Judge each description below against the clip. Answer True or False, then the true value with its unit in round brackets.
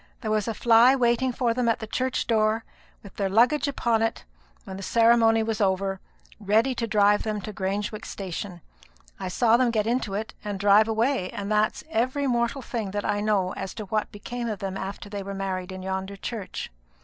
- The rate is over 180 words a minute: True (205 wpm)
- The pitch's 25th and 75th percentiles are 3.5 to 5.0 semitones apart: False (2.9 semitones)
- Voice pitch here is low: False (215 Hz)